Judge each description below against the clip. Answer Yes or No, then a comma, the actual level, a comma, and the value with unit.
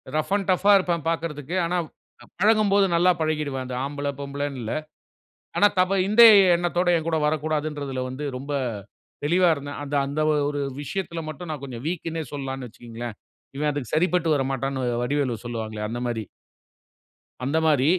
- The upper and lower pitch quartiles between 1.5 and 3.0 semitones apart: No, average, 4.0 semitones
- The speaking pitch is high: No, medium, 145 Hz